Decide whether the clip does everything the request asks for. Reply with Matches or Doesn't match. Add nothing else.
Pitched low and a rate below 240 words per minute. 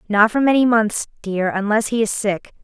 Doesn't match